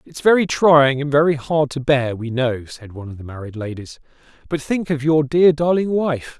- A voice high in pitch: No, medium, 140 Hz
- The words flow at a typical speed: No, fast, 215 wpm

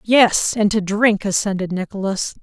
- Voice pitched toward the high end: Yes, high, 205 Hz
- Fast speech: No, average, 150 wpm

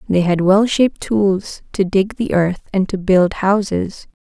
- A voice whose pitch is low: No, high, 195 Hz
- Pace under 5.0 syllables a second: Yes, 4.0 syllables/s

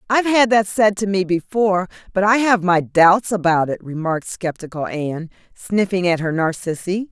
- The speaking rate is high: No, average, 175 wpm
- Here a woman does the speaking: Yes, female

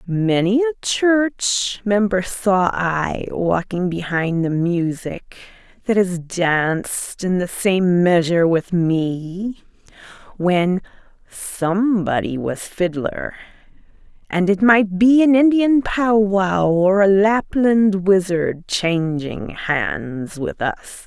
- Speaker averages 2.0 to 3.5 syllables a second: Yes, 3.2 syllables/s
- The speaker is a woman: Yes, female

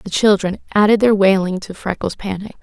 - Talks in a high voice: Yes, high, 200 Hz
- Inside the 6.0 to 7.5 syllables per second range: No, 5.4 syllables/s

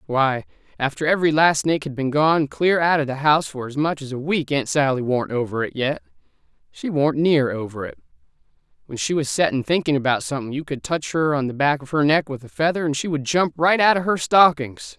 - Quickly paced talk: Yes, fast, 235 wpm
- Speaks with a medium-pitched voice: Yes, medium, 150 Hz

